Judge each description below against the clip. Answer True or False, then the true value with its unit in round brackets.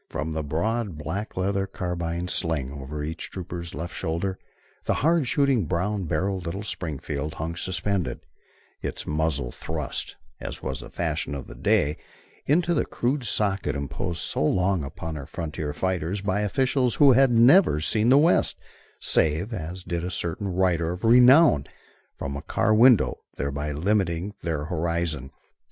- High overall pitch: False (90 Hz)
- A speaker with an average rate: True (155 wpm)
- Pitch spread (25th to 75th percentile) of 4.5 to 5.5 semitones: True (5.0 semitones)